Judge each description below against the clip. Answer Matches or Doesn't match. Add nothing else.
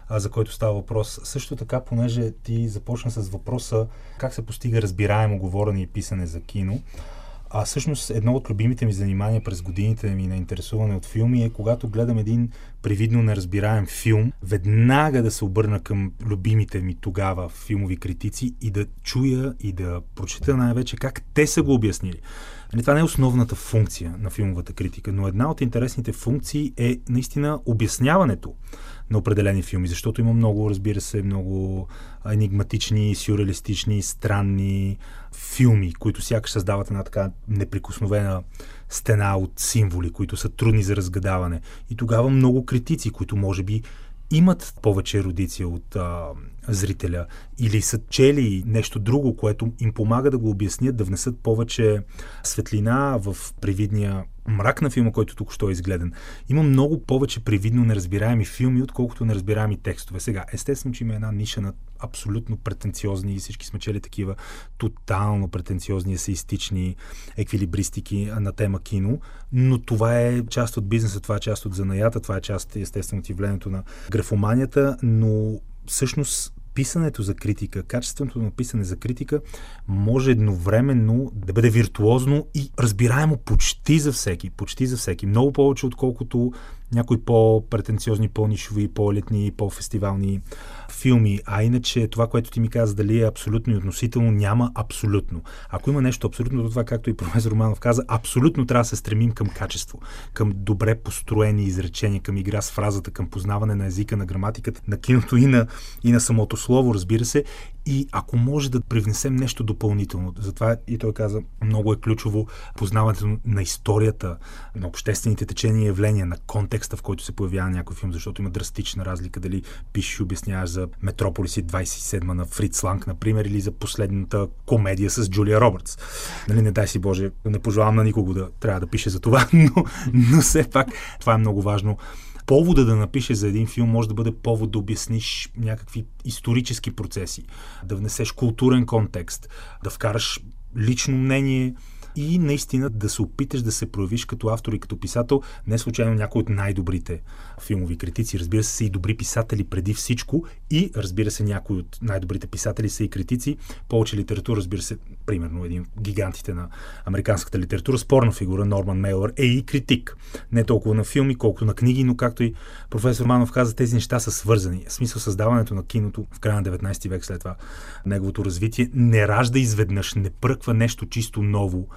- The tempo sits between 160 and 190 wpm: Matches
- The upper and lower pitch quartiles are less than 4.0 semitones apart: Matches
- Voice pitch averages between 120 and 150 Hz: Doesn't match